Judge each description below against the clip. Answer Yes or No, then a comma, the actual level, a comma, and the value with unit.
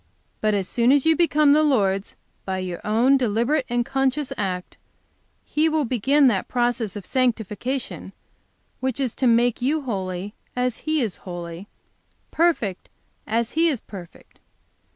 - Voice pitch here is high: Yes, high, 240 Hz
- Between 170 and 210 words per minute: No, average, 145 wpm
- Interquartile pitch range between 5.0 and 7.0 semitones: Yes, average, 5.3 semitones